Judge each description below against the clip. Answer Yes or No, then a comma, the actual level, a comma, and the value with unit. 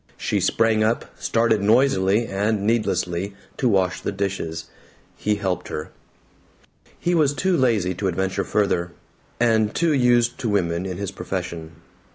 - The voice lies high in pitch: No, low, 105 Hz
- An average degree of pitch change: Yes, average, 3.9 semitones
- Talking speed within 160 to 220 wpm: No, average, 145 wpm